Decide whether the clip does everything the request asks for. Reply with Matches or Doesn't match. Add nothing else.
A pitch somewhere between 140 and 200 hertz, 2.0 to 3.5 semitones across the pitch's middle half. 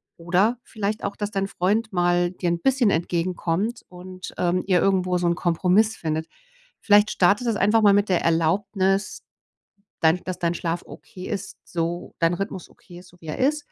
Matches